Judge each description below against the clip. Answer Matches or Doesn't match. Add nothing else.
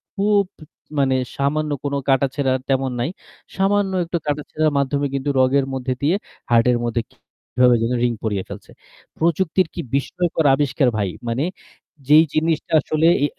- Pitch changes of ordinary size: Matches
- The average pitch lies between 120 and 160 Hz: Matches